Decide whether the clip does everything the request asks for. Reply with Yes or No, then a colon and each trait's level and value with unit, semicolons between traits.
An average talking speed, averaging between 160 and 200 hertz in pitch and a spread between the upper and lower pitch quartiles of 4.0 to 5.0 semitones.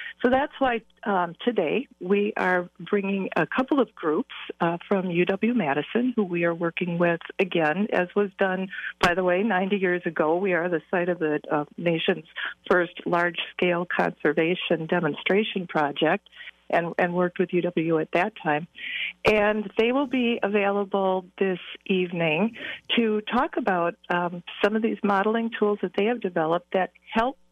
No: average, 165 wpm; medium, 185 Hz; average, 3.4 semitones